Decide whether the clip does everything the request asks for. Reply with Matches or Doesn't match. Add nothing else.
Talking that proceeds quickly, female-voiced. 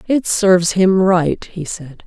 Doesn't match